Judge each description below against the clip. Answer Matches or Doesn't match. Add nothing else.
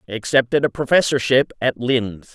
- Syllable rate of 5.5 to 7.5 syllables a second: Doesn't match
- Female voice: Doesn't match